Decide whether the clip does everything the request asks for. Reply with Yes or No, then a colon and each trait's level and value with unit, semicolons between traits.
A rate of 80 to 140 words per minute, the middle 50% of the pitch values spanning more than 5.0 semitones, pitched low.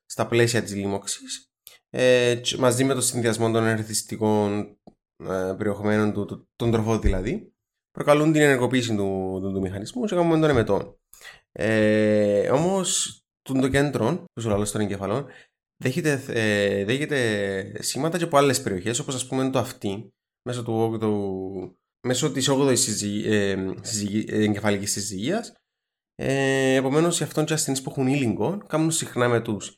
No: average, 135 wpm; average, 4.7 semitones; low, 115 Hz